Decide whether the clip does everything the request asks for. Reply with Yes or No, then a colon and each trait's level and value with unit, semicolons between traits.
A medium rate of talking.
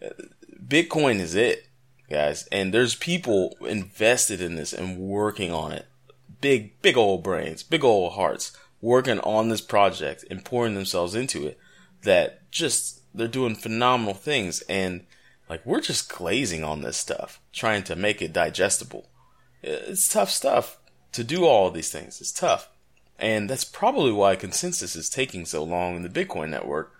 Yes: average, 160 wpm